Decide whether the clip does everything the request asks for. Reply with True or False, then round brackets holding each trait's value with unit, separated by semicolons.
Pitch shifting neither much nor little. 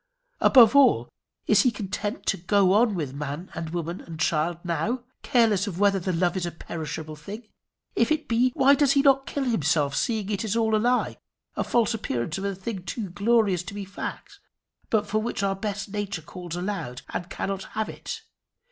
True (4.5 semitones)